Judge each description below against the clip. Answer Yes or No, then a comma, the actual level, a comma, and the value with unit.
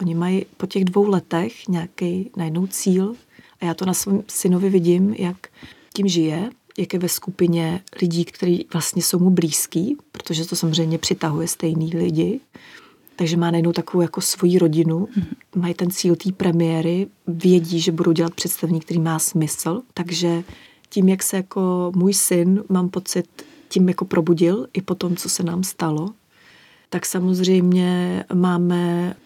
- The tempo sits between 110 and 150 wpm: No, average, 160 wpm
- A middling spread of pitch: No, narrow, 1.8 semitones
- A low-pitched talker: No, medium, 180 Hz